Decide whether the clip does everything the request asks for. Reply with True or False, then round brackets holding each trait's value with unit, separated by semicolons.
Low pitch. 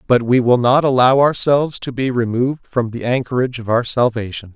True (125 Hz)